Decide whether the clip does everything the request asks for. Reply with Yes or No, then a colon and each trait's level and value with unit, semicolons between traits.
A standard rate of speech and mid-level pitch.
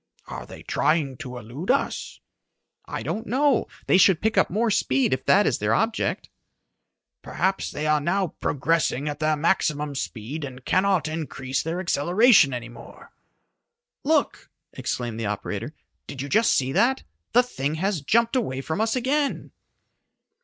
Yes: average, 155 wpm; medium, 160 Hz